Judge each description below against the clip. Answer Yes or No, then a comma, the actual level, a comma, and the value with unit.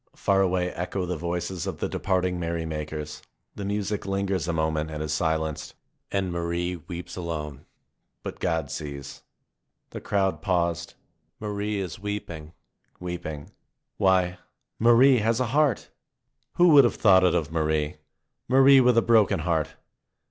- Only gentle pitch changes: No, average, 4.2 semitones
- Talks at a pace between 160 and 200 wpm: No, average, 145 wpm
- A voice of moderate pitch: No, very low, 90 Hz